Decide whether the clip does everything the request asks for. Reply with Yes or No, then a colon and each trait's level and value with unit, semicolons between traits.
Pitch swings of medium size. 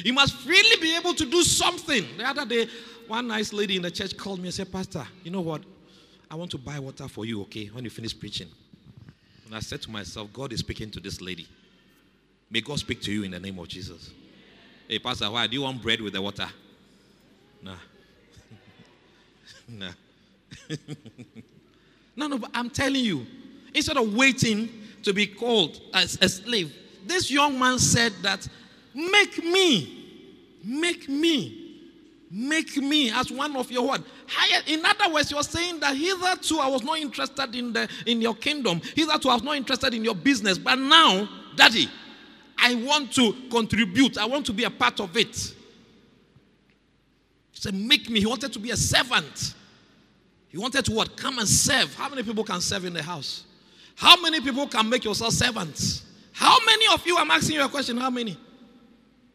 No: wide, 8.9 semitones